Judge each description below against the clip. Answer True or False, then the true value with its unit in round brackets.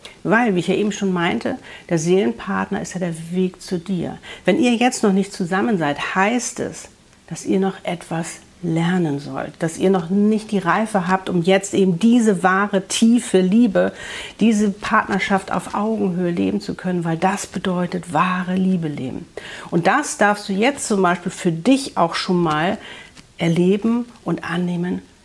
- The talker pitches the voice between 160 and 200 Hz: True (190 Hz)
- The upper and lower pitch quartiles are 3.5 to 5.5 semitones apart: False (2.9 semitones)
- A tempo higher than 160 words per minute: True (170 wpm)